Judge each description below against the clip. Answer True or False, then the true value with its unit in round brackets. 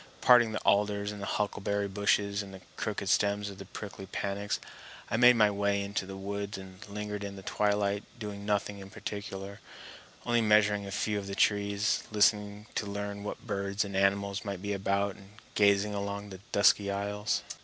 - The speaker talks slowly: False (180 wpm)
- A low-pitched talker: True (100 Hz)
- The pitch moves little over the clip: True (0.8 semitones)